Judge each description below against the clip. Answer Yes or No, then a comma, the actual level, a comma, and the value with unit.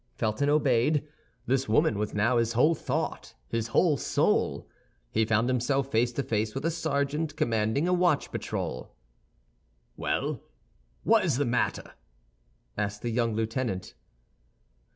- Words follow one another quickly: No, slow, 135 wpm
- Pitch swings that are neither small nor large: Yes, average, 4.5 semitones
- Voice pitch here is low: Yes, low, 125 Hz